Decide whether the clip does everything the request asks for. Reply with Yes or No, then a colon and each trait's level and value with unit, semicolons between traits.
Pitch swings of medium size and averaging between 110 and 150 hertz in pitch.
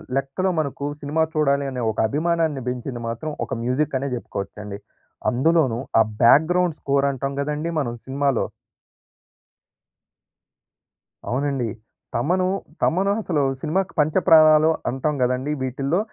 Yes: average, 3.5 semitones; medium, 140 Hz